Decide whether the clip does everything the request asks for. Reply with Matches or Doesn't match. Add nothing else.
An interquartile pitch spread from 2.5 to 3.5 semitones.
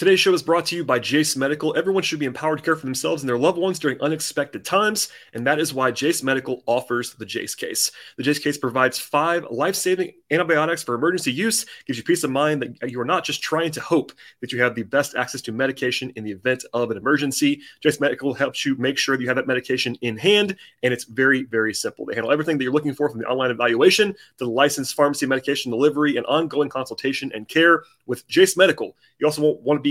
Doesn't match